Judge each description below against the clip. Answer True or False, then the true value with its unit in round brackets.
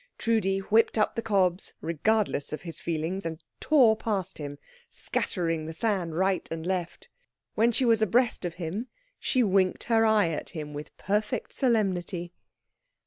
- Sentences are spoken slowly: False (155 wpm)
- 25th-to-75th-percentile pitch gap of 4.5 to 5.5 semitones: True (4.8 semitones)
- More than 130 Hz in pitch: True (190 Hz)